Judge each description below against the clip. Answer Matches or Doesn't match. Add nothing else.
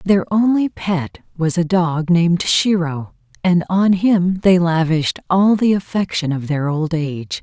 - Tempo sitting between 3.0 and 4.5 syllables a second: Matches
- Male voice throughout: Doesn't match